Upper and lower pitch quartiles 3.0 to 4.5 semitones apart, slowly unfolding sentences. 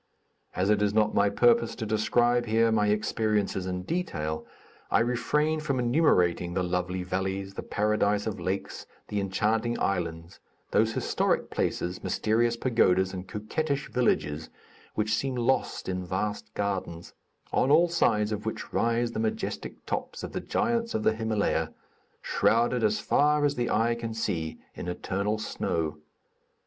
No: average, 3.9 semitones; average, 150 wpm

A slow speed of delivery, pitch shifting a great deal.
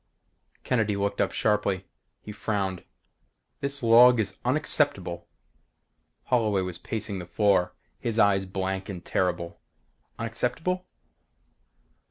No: slow, 105 wpm; average, 3.7 semitones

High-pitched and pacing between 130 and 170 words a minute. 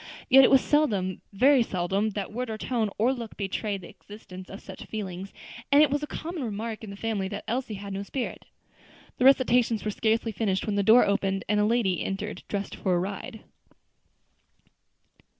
No: high, 215 Hz; average, 190 wpm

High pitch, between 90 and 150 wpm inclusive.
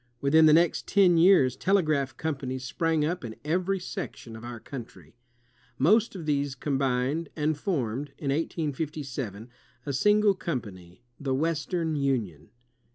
No: medium, 145 Hz; average, 145 wpm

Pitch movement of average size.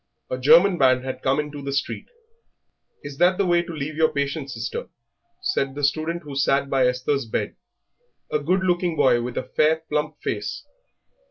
Yes: average, 3.5 semitones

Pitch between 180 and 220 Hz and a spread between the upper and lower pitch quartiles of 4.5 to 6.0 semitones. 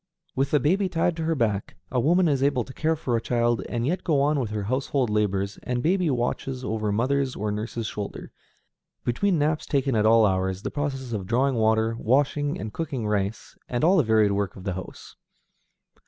No: low, 125 Hz; average, 5.1 semitones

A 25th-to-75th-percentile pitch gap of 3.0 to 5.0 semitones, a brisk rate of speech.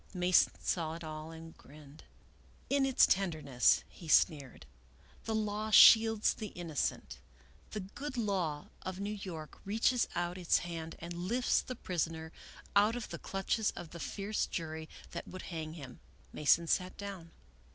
No: average, 4.5 semitones; average, 160 wpm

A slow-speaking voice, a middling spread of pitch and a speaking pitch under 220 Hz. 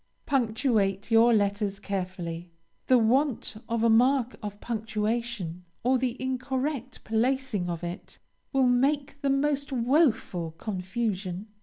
No: slow, 120 wpm; average, 4.7 semitones; high, 230 Hz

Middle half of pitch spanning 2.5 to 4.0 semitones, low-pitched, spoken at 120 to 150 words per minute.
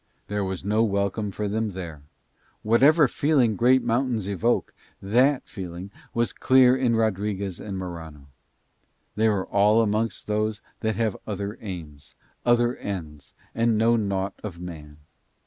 Yes: average, 3.5 semitones; low, 105 Hz; average, 140 wpm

